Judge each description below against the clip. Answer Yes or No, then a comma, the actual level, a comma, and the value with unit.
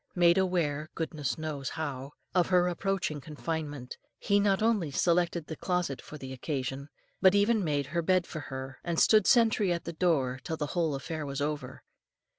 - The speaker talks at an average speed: Yes, average, 180 wpm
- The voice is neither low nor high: Yes, medium, 160 Hz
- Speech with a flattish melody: No, average, 3.9 semitones